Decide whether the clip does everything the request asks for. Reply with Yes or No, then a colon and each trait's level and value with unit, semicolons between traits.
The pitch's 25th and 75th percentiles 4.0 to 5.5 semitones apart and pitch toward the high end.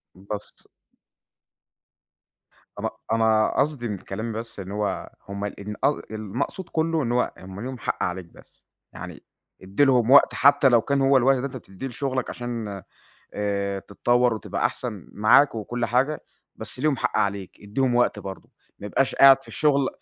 No: average, 4.8 semitones; low, 115 Hz